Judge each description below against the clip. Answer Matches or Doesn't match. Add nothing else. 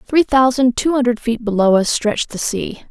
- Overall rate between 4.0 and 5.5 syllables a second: Matches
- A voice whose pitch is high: Matches